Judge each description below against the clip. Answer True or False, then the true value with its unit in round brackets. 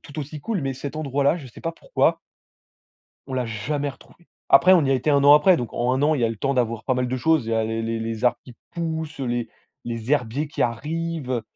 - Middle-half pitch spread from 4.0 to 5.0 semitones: True (4.3 semitones)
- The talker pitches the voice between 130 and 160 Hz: True (135 Hz)